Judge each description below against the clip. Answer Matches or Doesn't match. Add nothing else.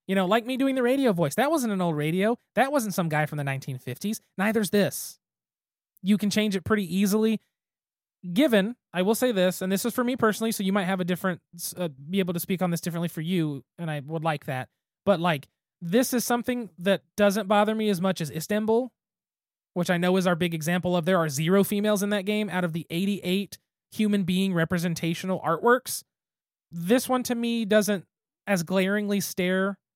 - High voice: Matches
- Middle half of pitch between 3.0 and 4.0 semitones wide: Matches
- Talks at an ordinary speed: Doesn't match